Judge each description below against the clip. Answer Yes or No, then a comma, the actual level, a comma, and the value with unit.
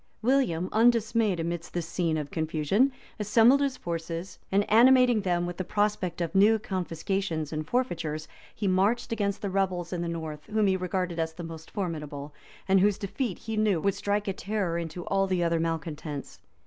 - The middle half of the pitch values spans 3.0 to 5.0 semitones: Yes, average, 3.9 semitones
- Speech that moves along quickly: No, average, 180 wpm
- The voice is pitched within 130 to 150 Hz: No, medium, 185 Hz